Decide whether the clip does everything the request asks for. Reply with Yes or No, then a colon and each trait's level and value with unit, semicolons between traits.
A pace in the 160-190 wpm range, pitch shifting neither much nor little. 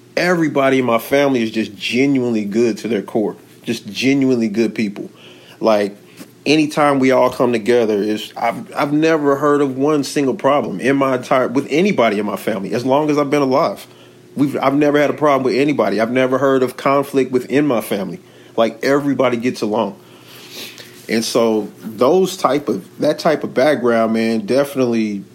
Yes: average, 180 wpm; average, 3.9 semitones